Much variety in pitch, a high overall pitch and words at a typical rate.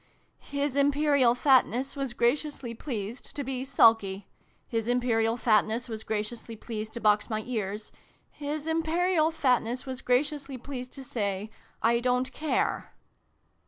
No: average, 4.1 semitones; very high, 250 Hz; average, 145 wpm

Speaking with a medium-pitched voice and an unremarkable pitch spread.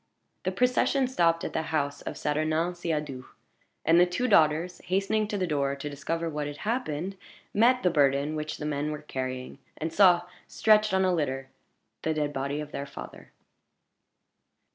Yes: medium, 155 Hz; average, 4.1 semitones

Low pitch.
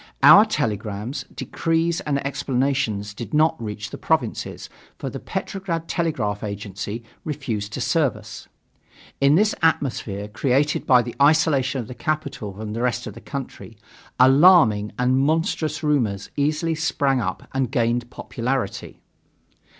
Yes: low, 130 Hz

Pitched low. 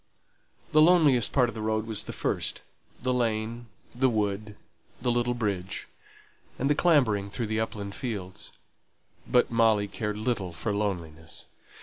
Yes: low, 110 Hz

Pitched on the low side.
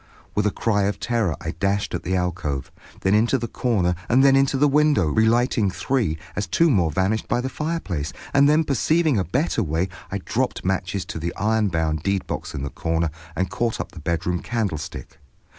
Yes: low, 100 Hz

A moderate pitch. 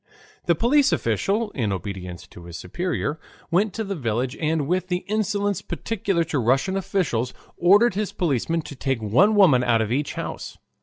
Yes: medium, 165 Hz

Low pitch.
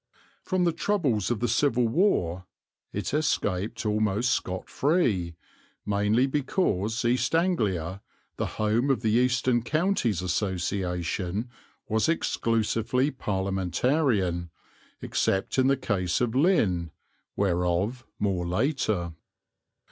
Yes: low, 110 Hz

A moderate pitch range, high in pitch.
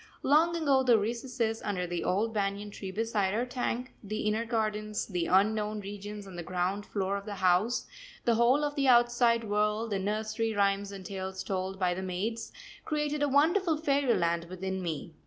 Yes: average, 3.8 semitones; high, 210 Hz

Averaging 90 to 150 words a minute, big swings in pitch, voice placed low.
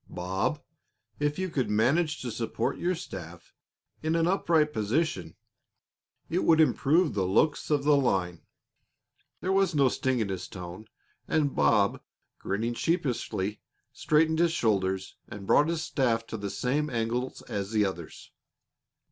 Yes: average, 145 wpm; wide, 7.7 semitones; low, 125 Hz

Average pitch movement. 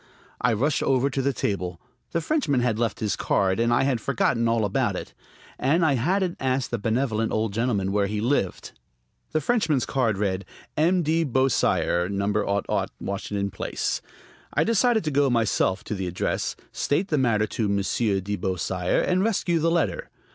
No: wide, 6.1 semitones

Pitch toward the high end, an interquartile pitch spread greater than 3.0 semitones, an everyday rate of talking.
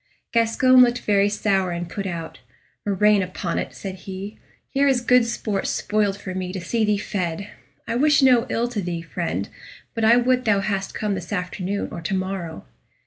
Yes: high, 200 Hz; average, 3.7 semitones; average, 190 wpm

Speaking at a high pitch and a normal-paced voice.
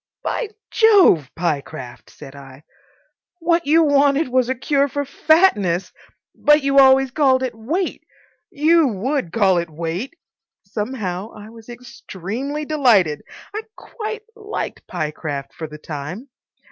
No: very high, 250 Hz; slow, 130 wpm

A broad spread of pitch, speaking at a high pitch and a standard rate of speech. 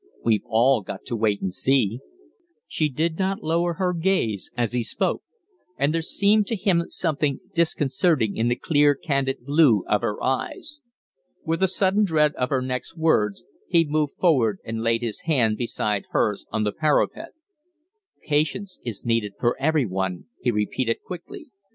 No: wide, 6.5 semitones; medium, 140 Hz; average, 165 wpm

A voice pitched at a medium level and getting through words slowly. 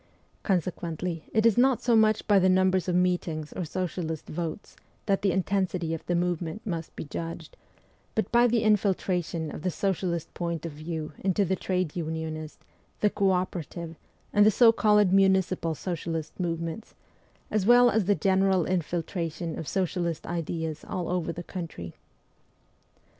No: medium, 180 Hz; average, 155 wpm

